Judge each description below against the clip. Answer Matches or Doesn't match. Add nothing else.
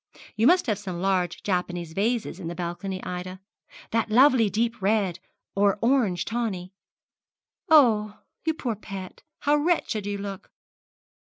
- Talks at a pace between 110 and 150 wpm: Matches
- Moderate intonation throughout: Matches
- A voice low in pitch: Doesn't match